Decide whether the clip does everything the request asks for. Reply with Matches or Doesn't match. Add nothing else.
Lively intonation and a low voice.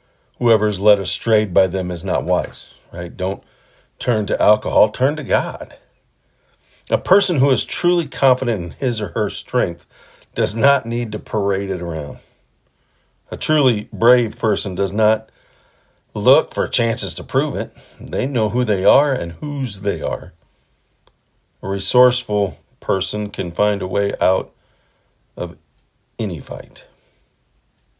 Doesn't match